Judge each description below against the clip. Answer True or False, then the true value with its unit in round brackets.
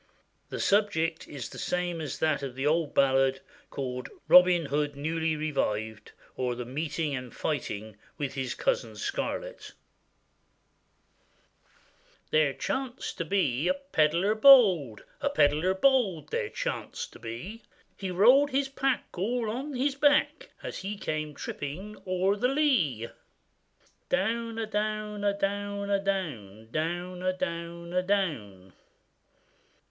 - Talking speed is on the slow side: True (130 wpm)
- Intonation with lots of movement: True (6.7 semitones)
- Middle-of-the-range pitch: True (180 Hz)